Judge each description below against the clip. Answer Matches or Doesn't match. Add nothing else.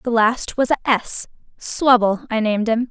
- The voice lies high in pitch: Matches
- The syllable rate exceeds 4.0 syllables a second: Matches